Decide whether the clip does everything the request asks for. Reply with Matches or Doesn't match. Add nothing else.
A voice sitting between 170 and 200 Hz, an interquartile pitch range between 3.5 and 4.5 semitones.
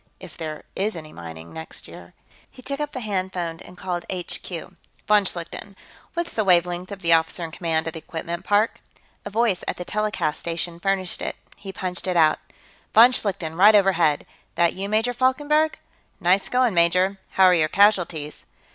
Matches